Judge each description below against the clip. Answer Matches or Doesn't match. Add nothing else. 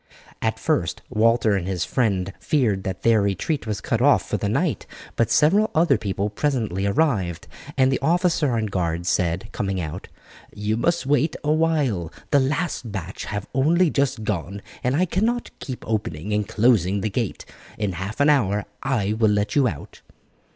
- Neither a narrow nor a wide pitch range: Doesn't match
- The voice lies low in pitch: Matches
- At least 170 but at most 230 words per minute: Matches